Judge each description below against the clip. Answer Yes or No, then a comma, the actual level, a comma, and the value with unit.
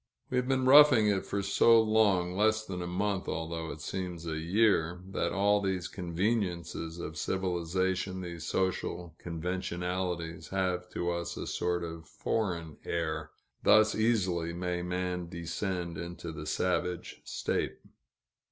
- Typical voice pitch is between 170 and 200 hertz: No, very low, 90 Hz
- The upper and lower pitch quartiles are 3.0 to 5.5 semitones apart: No, narrow, 2.4 semitones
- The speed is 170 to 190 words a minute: No, average, 140 wpm